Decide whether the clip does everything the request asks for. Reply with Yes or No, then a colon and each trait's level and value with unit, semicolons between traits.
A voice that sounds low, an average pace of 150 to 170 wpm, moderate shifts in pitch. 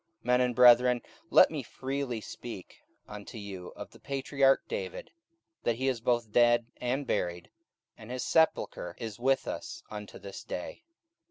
Yes: low, 120 Hz; average, 160 wpm; average, 3.8 semitones